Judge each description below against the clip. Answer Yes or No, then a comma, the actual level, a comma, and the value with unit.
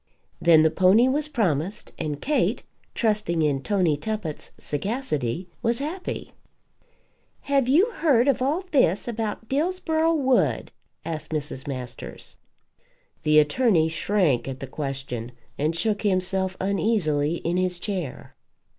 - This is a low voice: No, high, 190 Hz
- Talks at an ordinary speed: No, slow, 125 wpm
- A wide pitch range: Yes, wide, 8.2 semitones